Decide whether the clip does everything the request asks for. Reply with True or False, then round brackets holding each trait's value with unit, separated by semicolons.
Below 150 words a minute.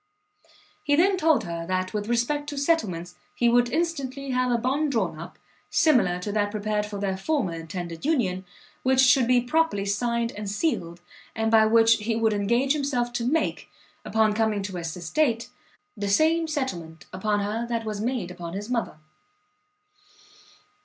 False (165 wpm)